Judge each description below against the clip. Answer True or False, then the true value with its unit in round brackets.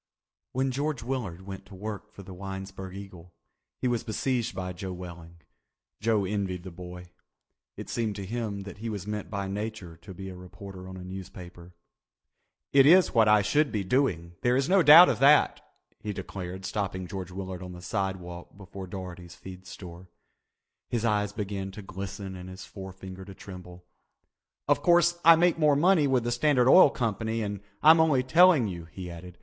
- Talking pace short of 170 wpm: False (185 wpm)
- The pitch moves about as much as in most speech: True (4.5 semitones)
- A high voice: False (100 Hz)